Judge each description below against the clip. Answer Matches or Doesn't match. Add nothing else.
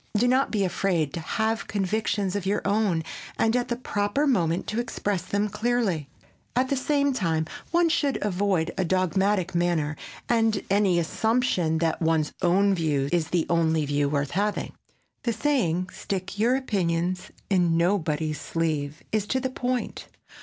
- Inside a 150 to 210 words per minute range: Matches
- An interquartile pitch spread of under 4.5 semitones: Doesn't match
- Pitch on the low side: Doesn't match